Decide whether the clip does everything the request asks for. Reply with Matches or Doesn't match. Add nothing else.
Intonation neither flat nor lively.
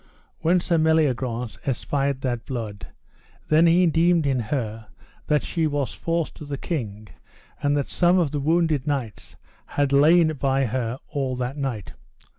Matches